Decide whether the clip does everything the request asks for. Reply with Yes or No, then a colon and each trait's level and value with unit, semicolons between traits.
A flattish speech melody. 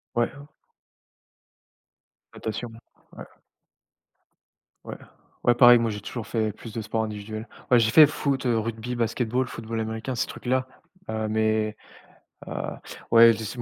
Yes: narrow, 1.8 semitones